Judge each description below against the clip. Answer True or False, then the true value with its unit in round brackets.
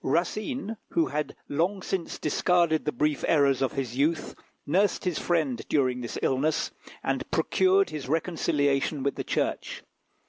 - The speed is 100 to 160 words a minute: True (145 wpm)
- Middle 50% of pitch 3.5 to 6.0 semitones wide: True (4.4 semitones)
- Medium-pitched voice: True (155 Hz)